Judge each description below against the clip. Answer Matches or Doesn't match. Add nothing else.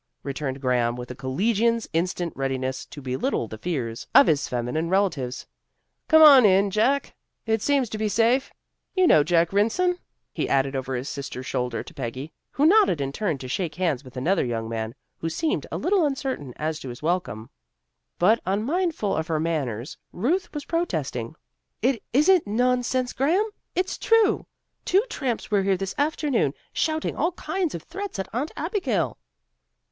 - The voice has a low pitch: Doesn't match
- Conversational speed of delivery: Matches